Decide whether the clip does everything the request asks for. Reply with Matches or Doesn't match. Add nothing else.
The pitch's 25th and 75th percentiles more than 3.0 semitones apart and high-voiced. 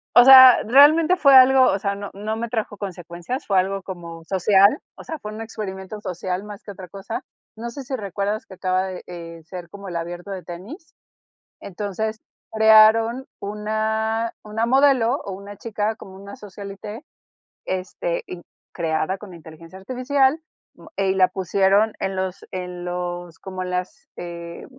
Matches